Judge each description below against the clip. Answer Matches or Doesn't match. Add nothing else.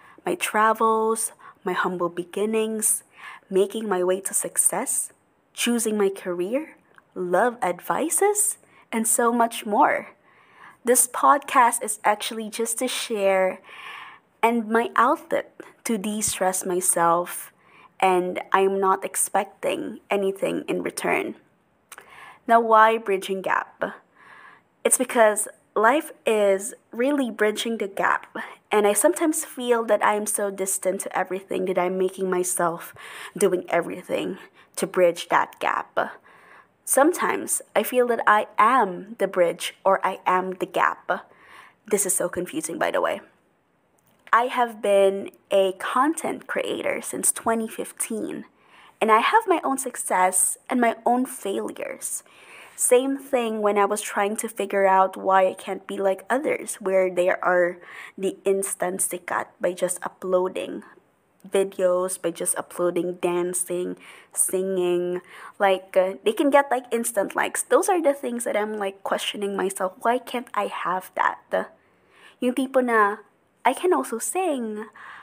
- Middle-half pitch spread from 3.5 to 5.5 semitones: Matches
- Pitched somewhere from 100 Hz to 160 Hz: Doesn't match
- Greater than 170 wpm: Doesn't match